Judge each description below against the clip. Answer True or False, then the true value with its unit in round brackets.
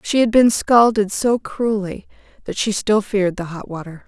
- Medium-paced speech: True (190 wpm)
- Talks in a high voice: True (205 Hz)